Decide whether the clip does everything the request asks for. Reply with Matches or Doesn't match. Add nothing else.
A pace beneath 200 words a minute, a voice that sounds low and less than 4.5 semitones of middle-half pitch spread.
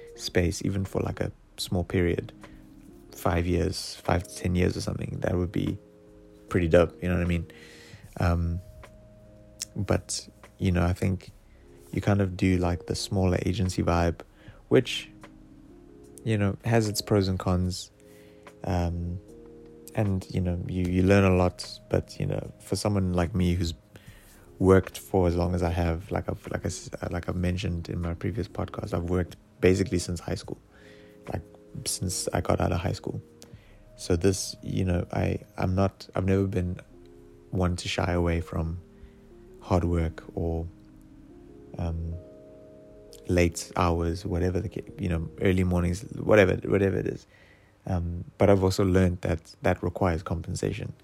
Matches